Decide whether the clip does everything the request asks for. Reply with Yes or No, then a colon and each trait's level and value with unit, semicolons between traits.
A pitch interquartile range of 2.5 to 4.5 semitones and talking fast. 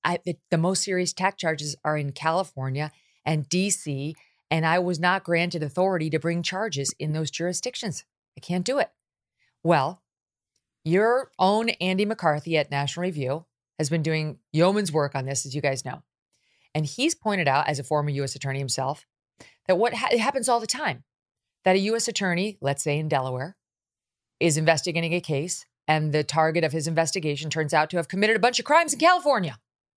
No: average, 4.0 semitones; average, 180 wpm